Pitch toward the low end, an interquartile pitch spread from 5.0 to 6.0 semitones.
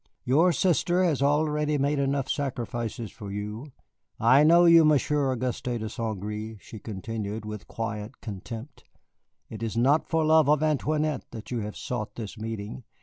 Yes: low, 120 Hz; wide, 5.4 semitones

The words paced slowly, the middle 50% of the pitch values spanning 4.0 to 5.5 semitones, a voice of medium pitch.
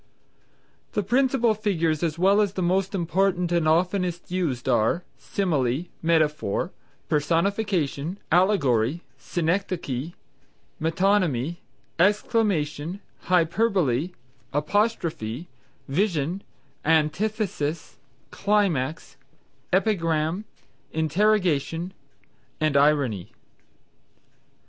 Yes: slow, 75 wpm; average, 4.5 semitones; medium, 170 Hz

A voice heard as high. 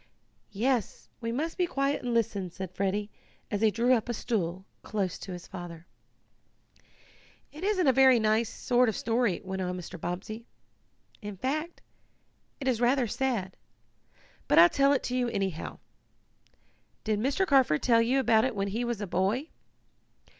Yes: high, 225 Hz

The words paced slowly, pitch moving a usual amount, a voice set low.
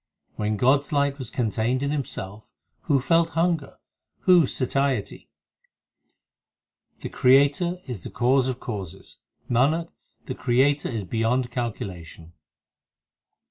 Yes: slow, 115 wpm; average, 4.0 semitones; low, 130 Hz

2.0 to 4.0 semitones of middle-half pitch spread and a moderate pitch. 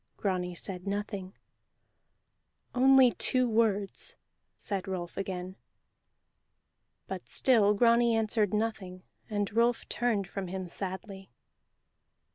No: average, 3.3 semitones; high, 200 Hz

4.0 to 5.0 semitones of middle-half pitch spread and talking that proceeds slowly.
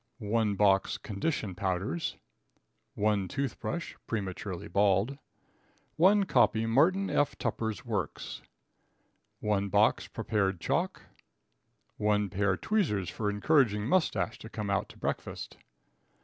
Yes: average, 4.3 semitones; slow, 105 wpm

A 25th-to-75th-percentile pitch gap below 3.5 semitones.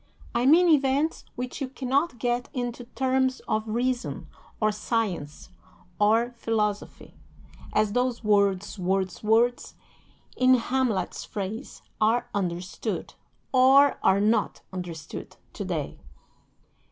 No: average, 3.8 semitones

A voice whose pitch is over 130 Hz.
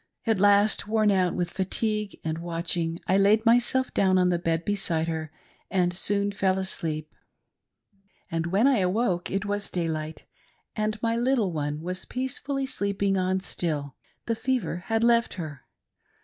Yes: high, 190 Hz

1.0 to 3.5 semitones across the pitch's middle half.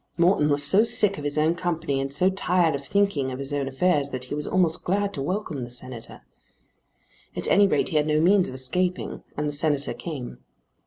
No: average, 4.7 semitones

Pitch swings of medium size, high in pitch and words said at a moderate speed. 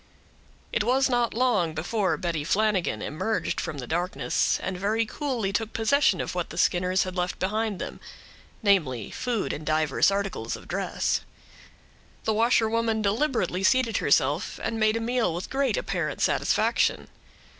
Yes: average, 4.4 semitones; high, 210 Hz; average, 150 wpm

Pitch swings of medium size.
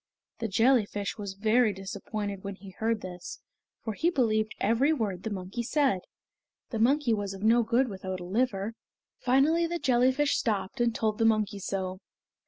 Yes: average, 3.9 semitones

